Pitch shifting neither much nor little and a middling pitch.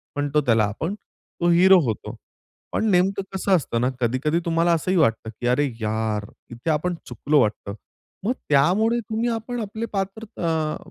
No: wide, 7.9 semitones; medium, 160 Hz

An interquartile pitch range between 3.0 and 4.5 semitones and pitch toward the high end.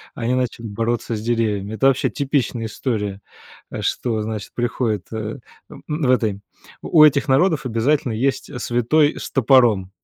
No: average, 3.5 semitones; low, 120 Hz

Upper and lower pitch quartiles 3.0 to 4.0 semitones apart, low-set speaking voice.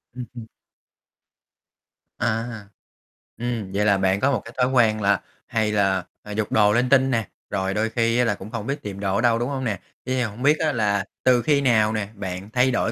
Yes: average, 3.3 semitones; low, 110 Hz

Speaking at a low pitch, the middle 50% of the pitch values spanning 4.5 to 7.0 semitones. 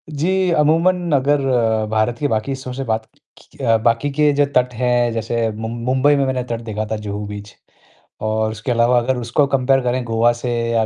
No: low, 120 Hz; average, 3.5 semitones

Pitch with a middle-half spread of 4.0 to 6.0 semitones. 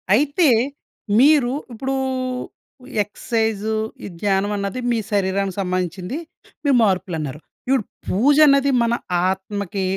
Yes: wide, 5.5 semitones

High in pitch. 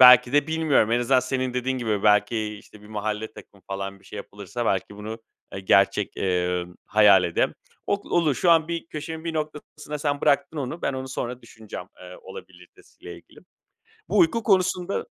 No: low, 125 Hz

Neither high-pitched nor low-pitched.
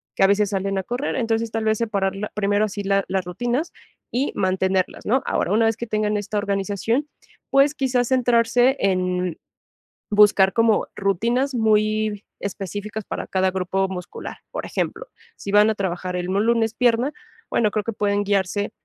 No: high, 210 Hz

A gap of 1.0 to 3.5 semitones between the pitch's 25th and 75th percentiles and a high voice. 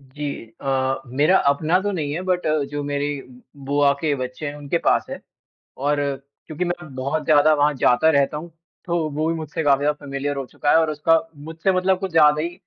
No: narrow, 2.6 semitones; medium, 150 Hz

